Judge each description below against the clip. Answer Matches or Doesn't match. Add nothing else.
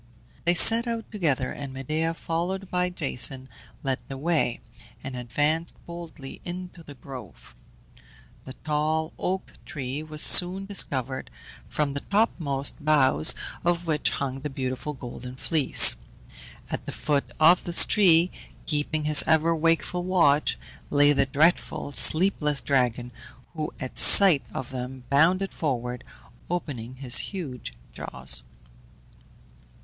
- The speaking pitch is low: Doesn't match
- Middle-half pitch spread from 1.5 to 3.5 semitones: Doesn't match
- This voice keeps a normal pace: Doesn't match